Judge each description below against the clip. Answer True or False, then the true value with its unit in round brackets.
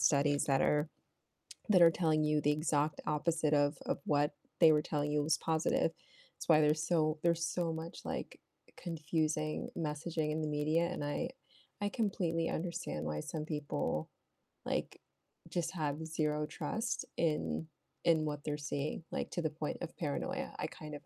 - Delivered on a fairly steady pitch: True (1.9 semitones)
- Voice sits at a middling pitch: True (155 Hz)